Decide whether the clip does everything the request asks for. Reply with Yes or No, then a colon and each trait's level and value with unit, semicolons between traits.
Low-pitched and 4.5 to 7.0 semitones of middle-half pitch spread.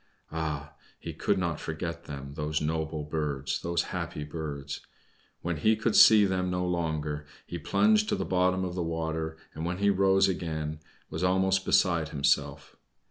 No: very low, 80 Hz; average, 3.4 semitones